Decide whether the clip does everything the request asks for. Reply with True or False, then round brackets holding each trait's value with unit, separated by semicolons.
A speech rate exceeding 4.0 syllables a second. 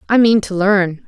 True (4.5 syllables/s)